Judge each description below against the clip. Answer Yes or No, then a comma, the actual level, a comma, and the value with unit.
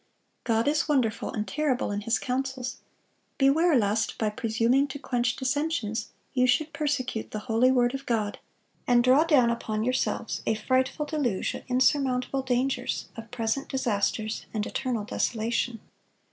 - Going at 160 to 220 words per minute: No, average, 145 wpm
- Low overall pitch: No, very high, 250 Hz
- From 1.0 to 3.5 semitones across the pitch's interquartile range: Yes, average, 3.2 semitones